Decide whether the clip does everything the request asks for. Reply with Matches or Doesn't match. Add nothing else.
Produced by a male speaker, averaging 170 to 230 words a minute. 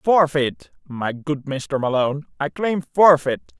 Doesn't match